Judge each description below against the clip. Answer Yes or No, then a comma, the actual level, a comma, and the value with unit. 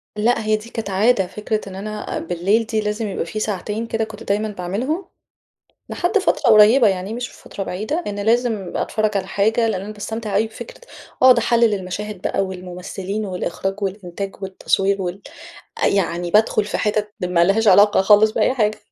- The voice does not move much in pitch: Yes, narrow, 2.3 semitones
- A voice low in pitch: No, high, 210 Hz